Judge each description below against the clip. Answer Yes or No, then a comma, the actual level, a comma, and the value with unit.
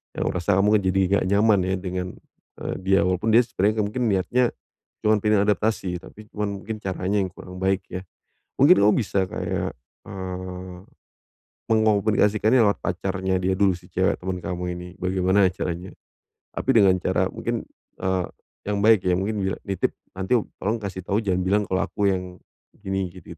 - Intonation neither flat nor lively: No, narrow, 2.2 semitones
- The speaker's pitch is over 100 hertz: No, very low, 95 Hz